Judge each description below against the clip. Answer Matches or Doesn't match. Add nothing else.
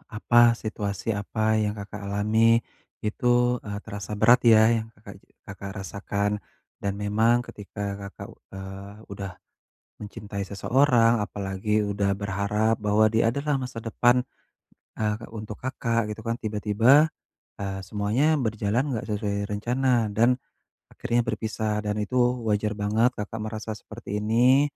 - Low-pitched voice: Matches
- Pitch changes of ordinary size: Doesn't match